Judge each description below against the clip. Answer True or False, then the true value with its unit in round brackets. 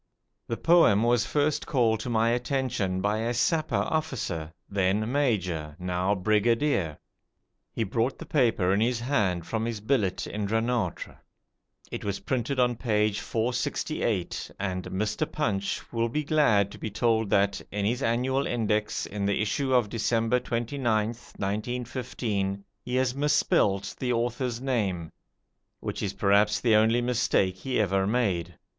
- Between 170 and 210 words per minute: False (145 wpm)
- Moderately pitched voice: False (110 Hz)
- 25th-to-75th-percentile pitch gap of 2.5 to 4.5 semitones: True (3.7 semitones)